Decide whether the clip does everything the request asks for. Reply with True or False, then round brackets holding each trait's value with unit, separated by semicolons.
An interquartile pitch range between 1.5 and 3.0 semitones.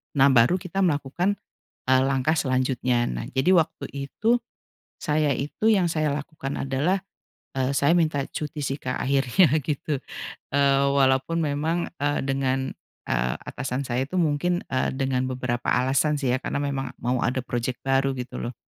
True (2.7 semitones)